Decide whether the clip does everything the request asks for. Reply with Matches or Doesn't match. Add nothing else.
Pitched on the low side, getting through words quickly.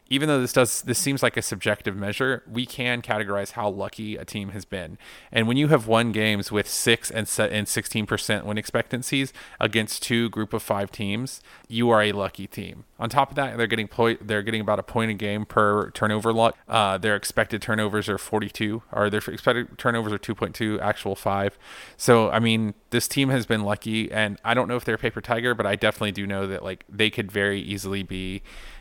Matches